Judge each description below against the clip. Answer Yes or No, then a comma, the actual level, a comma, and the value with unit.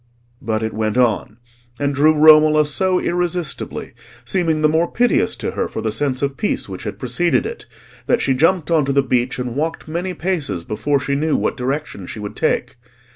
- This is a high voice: No, medium, 145 Hz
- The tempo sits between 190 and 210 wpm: Yes, average, 195 wpm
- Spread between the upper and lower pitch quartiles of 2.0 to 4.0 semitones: No, average, 4.7 semitones